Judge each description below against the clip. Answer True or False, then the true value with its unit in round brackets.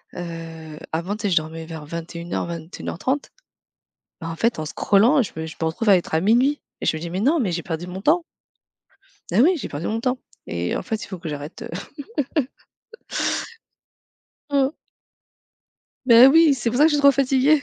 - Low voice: False (190 Hz)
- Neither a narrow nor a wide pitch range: False (8.1 semitones)